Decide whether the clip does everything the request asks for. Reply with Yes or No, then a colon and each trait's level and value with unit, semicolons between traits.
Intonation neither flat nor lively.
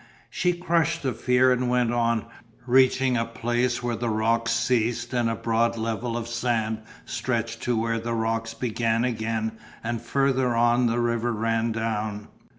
No: narrow, 1.4 semitones